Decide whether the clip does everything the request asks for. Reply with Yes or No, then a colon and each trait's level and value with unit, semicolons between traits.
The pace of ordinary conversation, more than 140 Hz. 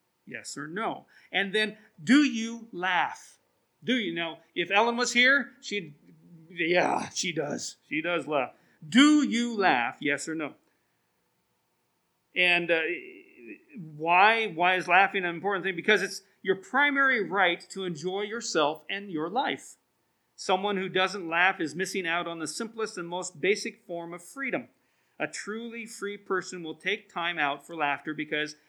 Yes: average, 155 wpm; high, 190 Hz